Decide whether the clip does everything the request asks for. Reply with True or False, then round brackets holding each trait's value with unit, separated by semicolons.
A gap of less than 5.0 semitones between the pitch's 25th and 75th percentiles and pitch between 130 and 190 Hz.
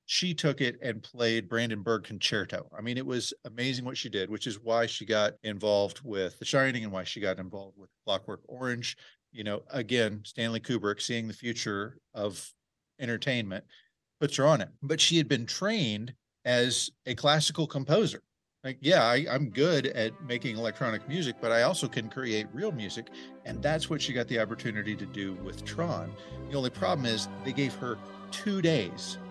False (4.3 semitones; 120 Hz)